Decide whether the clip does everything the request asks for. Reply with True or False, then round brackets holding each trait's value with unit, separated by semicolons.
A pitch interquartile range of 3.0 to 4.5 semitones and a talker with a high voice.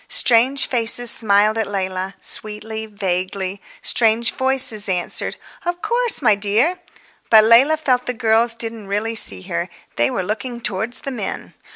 True (3.4 semitones; 220 Hz)